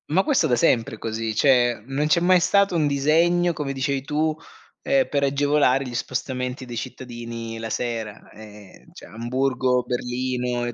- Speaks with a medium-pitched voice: No, low, 130 Hz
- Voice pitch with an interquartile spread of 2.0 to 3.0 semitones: No, average, 3.7 semitones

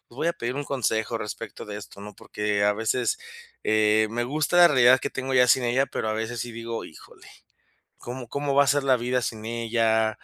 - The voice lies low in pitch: Yes, low, 120 Hz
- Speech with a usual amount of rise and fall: Yes, average, 3.1 semitones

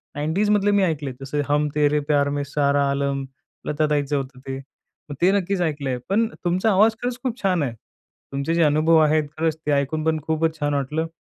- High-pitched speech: No, medium, 150 Hz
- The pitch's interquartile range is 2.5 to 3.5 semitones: Yes, average, 2.9 semitones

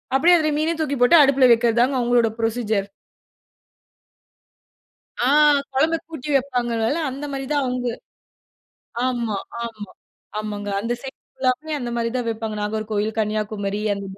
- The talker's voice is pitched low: No, high, 240 Hz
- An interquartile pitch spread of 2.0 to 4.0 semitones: Yes, average, 3.7 semitones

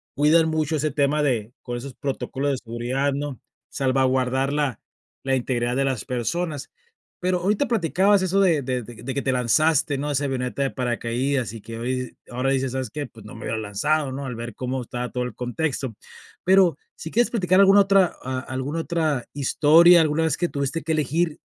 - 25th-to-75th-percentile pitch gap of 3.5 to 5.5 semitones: Yes, average, 4.1 semitones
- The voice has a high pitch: No, low, 135 Hz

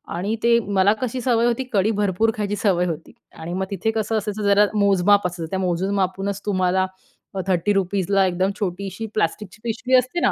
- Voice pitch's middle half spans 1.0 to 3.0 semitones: Yes, narrow, 2.5 semitones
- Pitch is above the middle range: Yes, high, 200 Hz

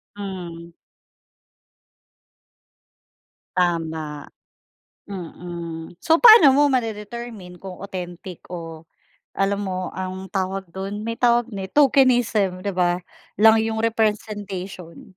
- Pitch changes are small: No, average, 3.9 semitones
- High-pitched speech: Yes, high, 195 Hz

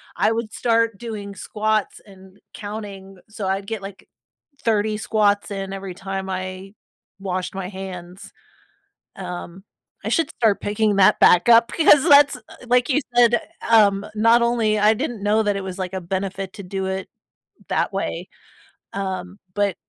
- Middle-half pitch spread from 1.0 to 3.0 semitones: Yes, narrow, 2.5 semitones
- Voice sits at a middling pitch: No, high, 200 Hz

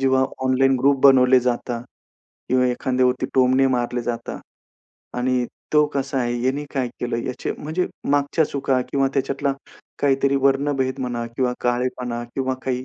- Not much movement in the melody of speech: Yes, narrow, 1.6 semitones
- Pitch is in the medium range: No, low, 130 Hz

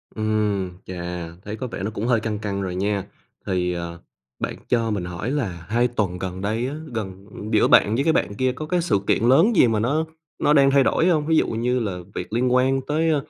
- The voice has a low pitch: Yes, low, 110 Hz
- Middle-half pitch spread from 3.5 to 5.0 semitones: No, wide, 5.6 semitones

